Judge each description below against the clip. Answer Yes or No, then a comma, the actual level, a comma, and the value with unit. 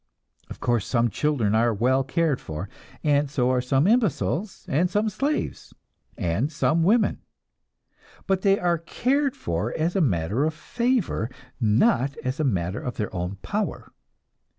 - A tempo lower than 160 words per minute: Yes, average, 150 wpm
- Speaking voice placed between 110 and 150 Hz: Yes, medium, 140 Hz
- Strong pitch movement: Yes, wide, 8.3 semitones